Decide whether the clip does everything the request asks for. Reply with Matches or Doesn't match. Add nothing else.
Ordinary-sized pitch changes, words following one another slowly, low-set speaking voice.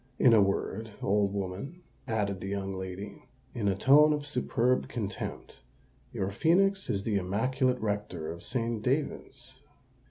Doesn't match